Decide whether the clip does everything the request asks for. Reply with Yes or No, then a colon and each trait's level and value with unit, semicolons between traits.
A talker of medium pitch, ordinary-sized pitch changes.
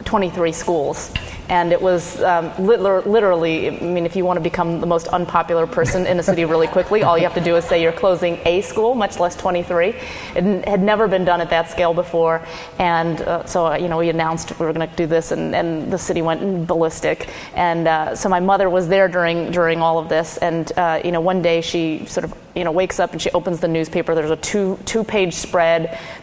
No: medium, 175 Hz; narrow, 1.7 semitones